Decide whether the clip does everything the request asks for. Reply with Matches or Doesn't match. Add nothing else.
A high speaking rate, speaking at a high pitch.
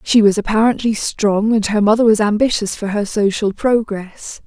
Doesn't match